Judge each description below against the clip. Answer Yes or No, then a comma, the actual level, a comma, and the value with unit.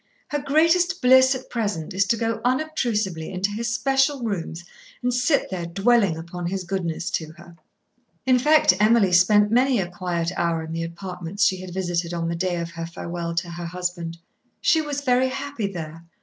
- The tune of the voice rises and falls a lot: Yes, wide, 6.5 semitones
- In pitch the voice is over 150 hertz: Yes, high, 190 Hz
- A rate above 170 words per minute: Yes, average, 185 wpm